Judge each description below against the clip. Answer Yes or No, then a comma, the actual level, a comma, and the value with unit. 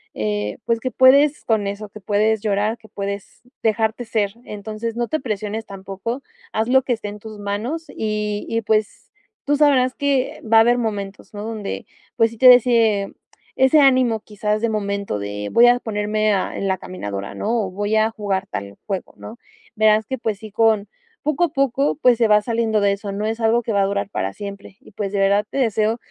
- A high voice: Yes, high, 215 Hz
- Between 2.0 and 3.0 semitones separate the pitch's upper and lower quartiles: Yes, narrow, 2.6 semitones